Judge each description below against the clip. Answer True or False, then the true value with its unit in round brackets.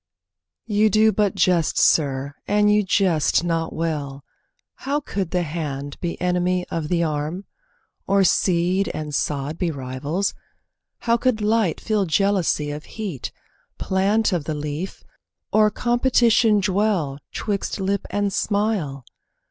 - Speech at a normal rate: False (130 wpm)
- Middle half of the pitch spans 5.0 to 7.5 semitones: True (5.3 semitones)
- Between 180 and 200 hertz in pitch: True (185 Hz)